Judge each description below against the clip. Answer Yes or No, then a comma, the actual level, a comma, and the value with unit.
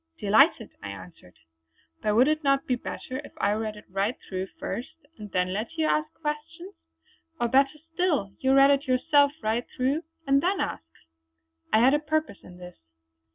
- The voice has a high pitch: Yes, very high, 260 Hz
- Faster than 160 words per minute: Yes, average, 180 wpm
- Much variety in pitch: Yes, wide, 6.2 semitones